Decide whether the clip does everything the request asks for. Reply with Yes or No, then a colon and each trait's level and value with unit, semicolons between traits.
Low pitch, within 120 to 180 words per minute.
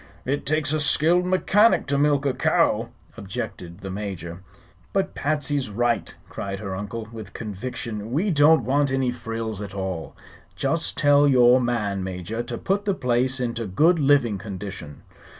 Yes: low, 120 Hz; average, 155 wpm